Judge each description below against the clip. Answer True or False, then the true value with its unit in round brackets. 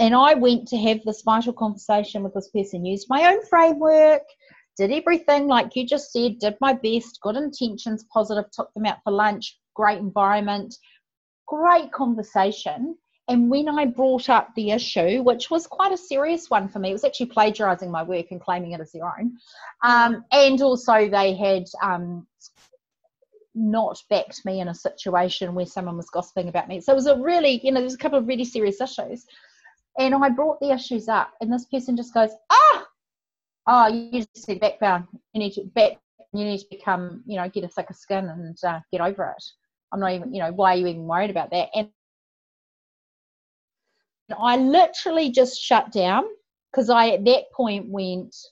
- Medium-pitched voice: False (225 Hz)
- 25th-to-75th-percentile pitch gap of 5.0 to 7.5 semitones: True (5.6 semitones)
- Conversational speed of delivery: True (195 wpm)